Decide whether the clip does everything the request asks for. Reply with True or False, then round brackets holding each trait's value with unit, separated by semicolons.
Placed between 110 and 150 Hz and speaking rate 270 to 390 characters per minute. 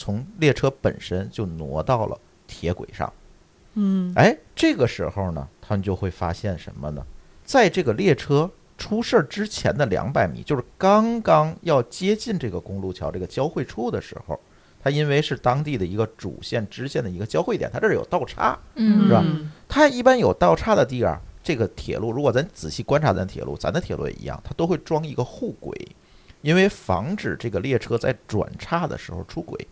True (135 Hz; 290 characters per minute)